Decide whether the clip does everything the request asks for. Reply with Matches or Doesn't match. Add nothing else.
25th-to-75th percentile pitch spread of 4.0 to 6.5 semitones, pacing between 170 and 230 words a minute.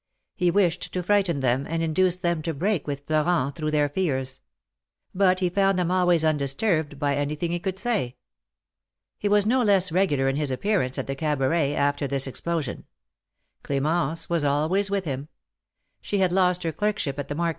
Matches